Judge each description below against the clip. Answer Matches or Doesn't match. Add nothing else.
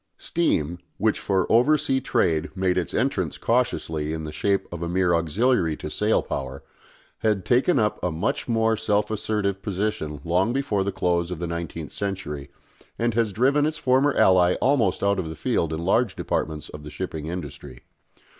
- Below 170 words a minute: Doesn't match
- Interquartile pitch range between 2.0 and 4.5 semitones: Doesn't match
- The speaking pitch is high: Doesn't match